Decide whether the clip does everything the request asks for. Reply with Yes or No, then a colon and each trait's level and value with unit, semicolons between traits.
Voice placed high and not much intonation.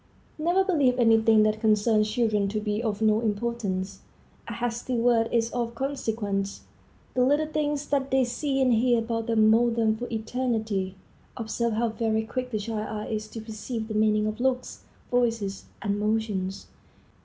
Yes: high, 225 Hz; narrow, 2.3 semitones